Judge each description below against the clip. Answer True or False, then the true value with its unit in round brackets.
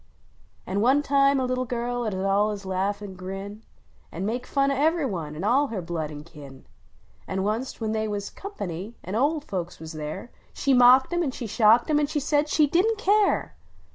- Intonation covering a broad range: True (6.5 semitones)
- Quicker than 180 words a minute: True (200 wpm)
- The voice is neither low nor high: False (225 Hz)